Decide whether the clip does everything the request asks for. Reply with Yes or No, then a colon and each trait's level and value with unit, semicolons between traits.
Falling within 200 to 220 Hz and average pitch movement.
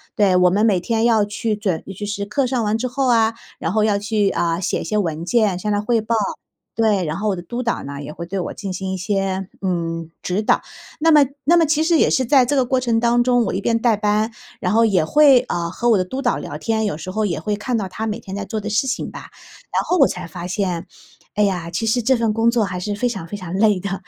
Yes: high, 210 Hz; average, 3.8 semitones